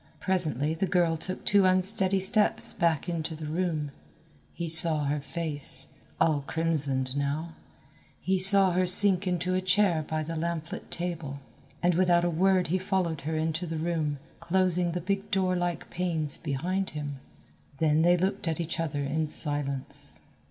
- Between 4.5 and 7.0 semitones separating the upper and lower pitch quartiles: No, average, 3.0 semitones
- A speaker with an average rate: Yes, average, 160 wpm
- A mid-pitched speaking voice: Yes, medium, 170 Hz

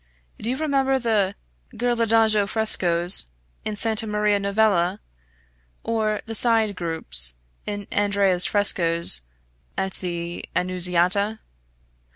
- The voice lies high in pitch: Yes, high, 205 Hz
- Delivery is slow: Yes, slow, 100 wpm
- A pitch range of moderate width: Yes, average, 3.5 semitones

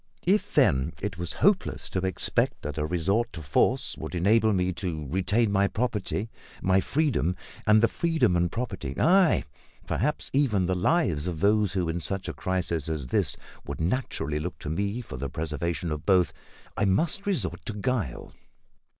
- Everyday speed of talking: Yes, average, 175 wpm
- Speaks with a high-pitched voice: No, very low, 95 Hz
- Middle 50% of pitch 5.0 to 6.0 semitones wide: Yes, wide, 5.5 semitones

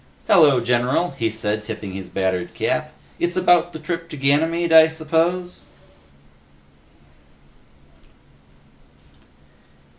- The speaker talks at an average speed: No, slow, 95 wpm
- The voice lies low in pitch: No, medium, 155 Hz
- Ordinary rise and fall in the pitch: No, wide, 7.0 semitones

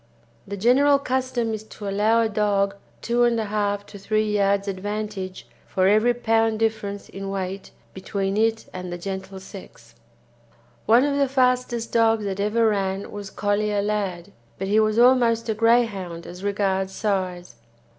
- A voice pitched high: Yes, high, 210 Hz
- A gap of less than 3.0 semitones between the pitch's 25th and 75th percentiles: Yes, narrow, 2.6 semitones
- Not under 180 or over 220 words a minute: No, average, 155 wpm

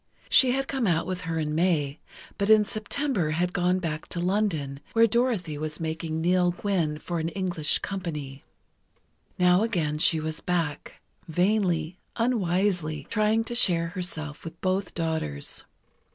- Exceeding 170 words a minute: No, average, 150 wpm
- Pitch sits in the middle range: Yes, medium, 175 Hz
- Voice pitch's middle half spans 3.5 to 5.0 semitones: Yes, average, 4.0 semitones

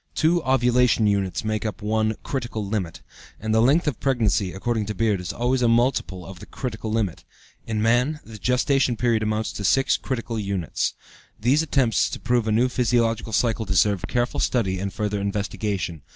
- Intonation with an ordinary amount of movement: Yes, average, 3.2 semitones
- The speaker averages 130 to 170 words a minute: No, average, 180 wpm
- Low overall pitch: Yes, low, 110 Hz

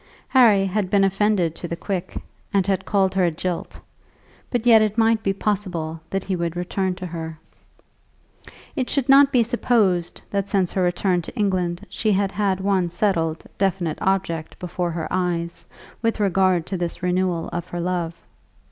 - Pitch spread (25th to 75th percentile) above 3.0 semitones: No, average, 2.7 semitones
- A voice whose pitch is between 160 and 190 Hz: Yes, medium, 185 Hz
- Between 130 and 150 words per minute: No, average, 175 wpm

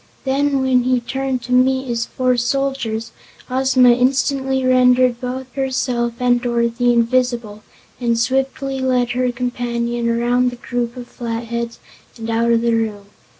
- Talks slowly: No, average, 145 wpm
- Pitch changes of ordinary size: No, narrow, 1.6 semitones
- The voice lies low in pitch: No, high, 245 Hz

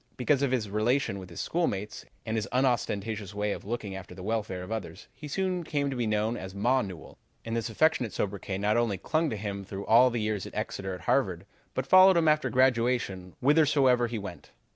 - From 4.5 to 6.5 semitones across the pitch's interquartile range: Yes, average, 4.8 semitones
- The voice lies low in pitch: Yes, low, 110 Hz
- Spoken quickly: Yes, fast, 210 wpm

